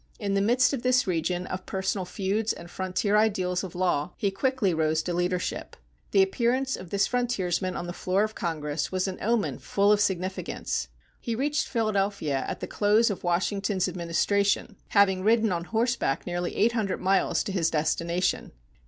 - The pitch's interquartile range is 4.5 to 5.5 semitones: No, average, 3.3 semitones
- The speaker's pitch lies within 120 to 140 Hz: No, high, 195 Hz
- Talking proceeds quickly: No, average, 175 wpm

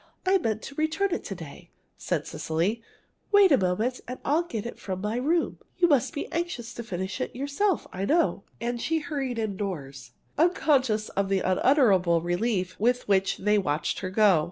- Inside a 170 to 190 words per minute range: Yes, average, 180 wpm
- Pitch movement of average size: No, wide, 7.2 semitones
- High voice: Yes, high, 230 Hz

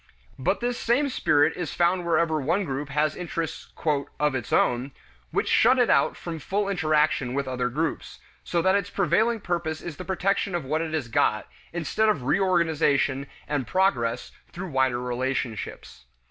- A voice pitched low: No, medium, 160 Hz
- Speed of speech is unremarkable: Yes, average, 165 wpm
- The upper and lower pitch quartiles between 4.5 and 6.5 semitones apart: Yes, wide, 5.6 semitones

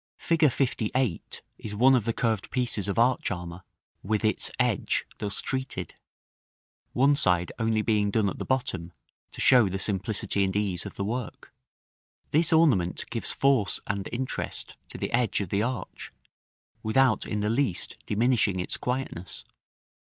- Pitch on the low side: Yes, low, 110 Hz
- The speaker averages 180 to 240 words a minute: No, average, 155 wpm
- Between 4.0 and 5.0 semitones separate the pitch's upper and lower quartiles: Yes, average, 4.5 semitones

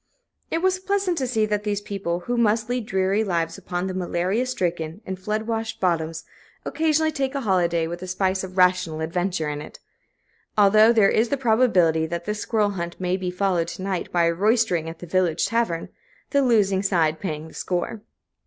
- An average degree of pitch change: Yes, average, 4.5 semitones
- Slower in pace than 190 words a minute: No, average, 195 wpm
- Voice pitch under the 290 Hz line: Yes, high, 190 Hz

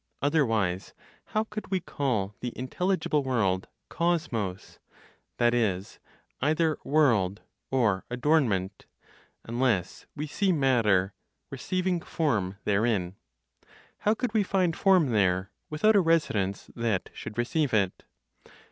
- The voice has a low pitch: Yes, low, 125 Hz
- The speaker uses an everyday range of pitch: No, wide, 8.4 semitones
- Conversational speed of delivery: No, slow, 110 wpm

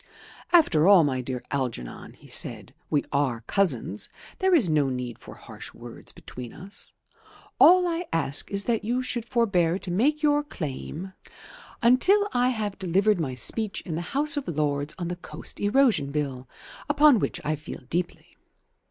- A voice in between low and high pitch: Yes, medium, 180 Hz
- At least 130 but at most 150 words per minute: No, average, 165 wpm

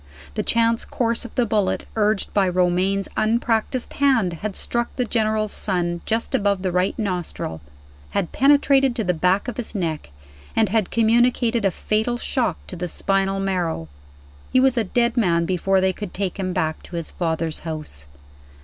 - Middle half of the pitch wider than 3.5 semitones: Yes, average, 4.3 semitones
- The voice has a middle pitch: No, high, 200 Hz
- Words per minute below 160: No, average, 175 wpm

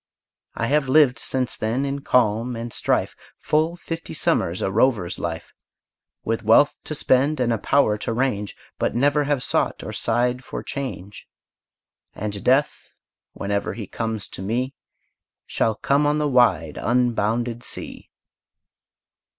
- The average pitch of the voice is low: Yes, low, 120 Hz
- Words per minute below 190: Yes, average, 140 wpm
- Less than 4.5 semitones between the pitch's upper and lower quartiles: Yes, average, 4.1 semitones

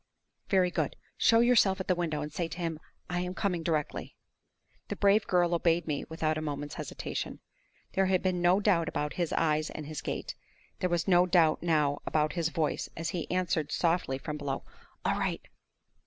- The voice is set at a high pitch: No, medium, 170 Hz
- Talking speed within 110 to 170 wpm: No, average, 190 wpm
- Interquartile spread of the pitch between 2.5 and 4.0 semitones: Yes, average, 2.8 semitones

